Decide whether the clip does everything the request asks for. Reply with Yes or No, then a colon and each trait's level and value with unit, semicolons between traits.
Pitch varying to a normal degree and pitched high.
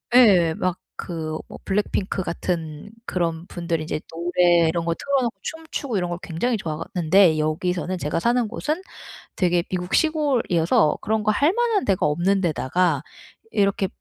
No: average, 4.4 semitones; medium, 180 Hz